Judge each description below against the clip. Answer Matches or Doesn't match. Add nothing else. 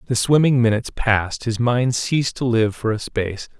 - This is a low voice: Matches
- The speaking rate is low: Doesn't match